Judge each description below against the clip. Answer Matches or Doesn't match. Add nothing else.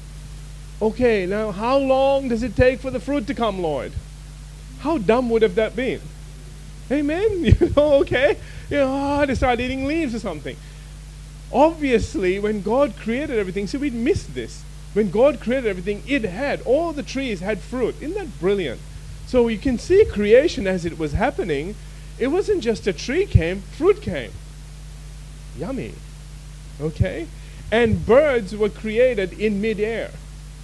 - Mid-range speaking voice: Doesn't match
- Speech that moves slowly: Doesn't match